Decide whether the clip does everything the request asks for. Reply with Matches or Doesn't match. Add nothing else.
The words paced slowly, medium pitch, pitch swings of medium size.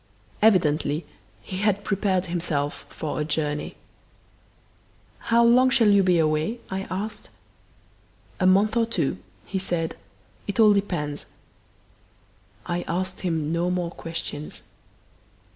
Matches